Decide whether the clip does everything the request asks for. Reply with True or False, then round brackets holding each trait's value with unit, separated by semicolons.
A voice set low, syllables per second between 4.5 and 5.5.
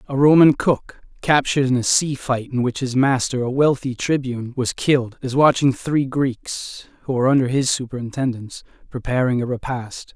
True (130 Hz; 5.2 syllables/s)